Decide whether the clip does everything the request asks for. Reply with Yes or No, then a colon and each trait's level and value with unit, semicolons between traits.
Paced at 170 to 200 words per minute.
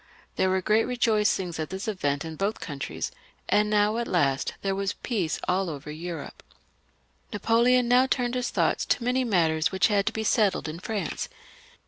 Yes: average, 175 wpm